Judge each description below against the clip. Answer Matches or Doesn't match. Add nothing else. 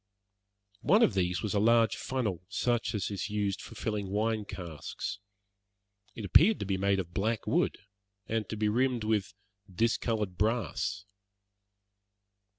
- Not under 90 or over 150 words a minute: Matches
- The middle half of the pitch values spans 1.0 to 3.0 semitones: Matches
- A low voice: Matches